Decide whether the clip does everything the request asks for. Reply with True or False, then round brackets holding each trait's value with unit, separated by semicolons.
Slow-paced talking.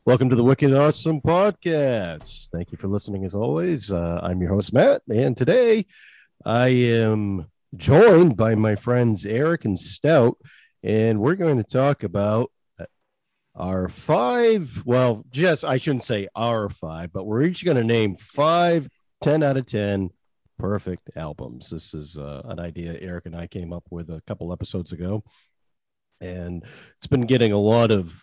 False (165 wpm)